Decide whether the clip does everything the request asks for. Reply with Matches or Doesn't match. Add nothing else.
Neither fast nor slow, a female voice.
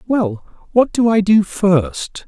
Doesn't match